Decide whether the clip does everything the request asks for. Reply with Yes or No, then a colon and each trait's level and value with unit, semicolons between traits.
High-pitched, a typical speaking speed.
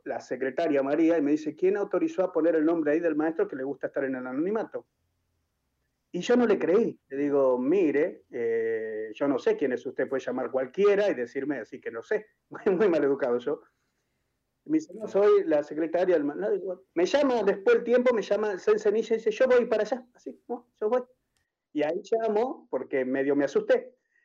No: high, 200 Hz; fast, 220 wpm